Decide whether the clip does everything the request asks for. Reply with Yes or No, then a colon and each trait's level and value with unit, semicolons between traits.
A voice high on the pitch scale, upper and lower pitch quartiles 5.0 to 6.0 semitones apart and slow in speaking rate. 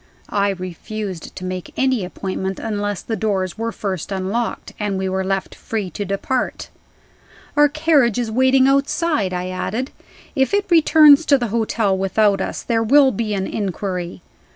No: high, 210 Hz; wide, 5.4 semitones; average, 160 wpm